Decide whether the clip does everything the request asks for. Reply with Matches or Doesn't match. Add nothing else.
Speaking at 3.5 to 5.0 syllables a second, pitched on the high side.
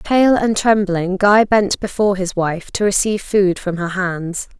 Matches